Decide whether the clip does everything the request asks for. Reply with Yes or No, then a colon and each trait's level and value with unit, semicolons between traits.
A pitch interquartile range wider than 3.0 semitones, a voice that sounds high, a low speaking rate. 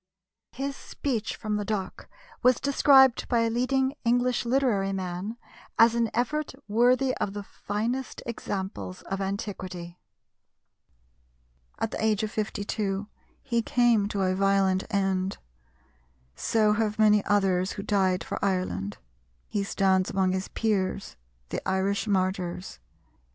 Yes: average, 3.5 semitones; high, 205 Hz; slow, 130 wpm